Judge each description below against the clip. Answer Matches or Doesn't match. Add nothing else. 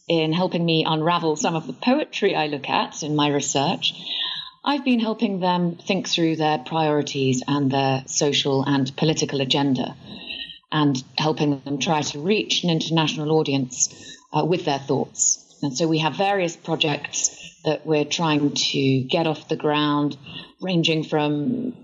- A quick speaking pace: Doesn't match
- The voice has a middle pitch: Matches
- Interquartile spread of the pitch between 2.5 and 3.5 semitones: Matches